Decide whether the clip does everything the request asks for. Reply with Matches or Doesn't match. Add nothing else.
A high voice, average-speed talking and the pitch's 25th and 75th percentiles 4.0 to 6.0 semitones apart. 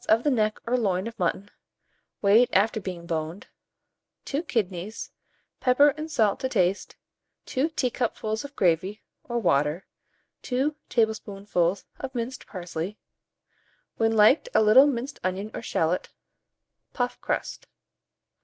Doesn't match